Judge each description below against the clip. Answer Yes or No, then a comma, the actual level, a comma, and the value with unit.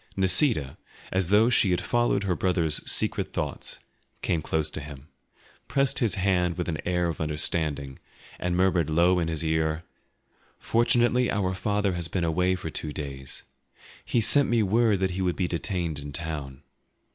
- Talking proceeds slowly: No, average, 170 wpm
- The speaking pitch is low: Yes, very low, 90 Hz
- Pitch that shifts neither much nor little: Yes, average, 3.9 semitones